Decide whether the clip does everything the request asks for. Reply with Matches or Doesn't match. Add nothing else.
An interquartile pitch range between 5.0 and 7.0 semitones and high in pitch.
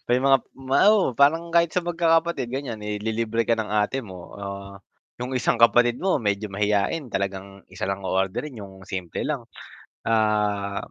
Doesn't match